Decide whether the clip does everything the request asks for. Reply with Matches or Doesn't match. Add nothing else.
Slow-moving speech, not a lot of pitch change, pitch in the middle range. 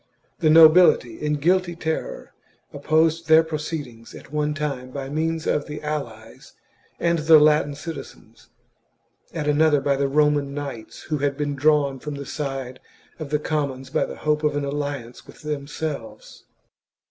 Doesn't match